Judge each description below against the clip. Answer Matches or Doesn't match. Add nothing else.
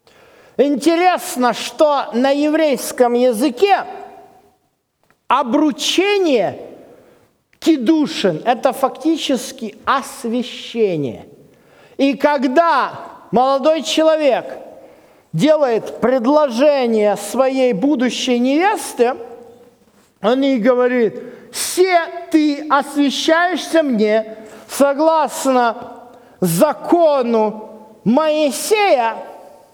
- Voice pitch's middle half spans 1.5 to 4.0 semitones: Doesn't match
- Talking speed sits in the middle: Doesn't match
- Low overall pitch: Doesn't match